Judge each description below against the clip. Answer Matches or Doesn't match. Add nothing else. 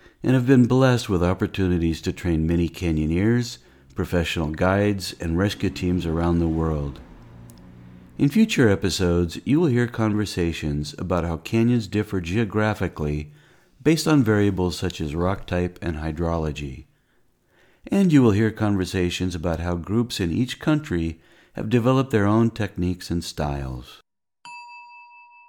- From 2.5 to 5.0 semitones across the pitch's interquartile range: Doesn't match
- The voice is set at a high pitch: Doesn't match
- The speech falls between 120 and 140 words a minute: Matches